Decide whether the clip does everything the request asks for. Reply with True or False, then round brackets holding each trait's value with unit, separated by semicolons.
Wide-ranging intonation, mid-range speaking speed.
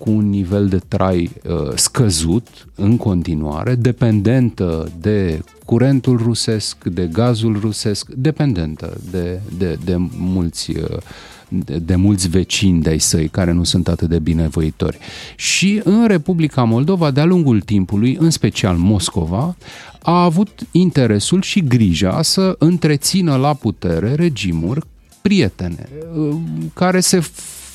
True (8.8 semitones; 130 wpm)